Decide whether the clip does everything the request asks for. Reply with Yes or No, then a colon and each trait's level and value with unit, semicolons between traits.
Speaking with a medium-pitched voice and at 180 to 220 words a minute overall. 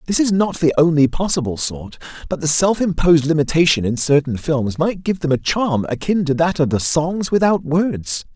Yes: medium, 160 Hz; average, 200 wpm